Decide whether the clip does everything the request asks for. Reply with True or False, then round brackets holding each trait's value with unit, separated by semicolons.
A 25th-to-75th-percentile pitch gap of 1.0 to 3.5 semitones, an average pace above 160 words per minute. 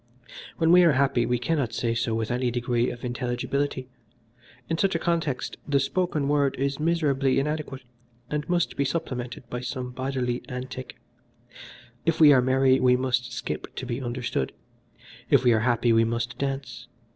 True (2.7 semitones; 170 wpm)